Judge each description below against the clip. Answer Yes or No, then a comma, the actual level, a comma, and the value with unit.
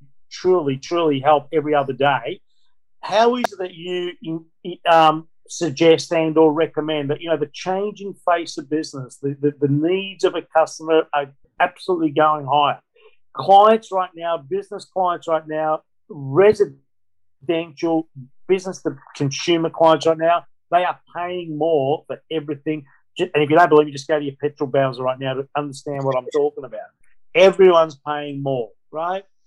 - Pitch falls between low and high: Yes, medium, 160 Hz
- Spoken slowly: No, average, 160 wpm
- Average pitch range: Yes, average, 3.4 semitones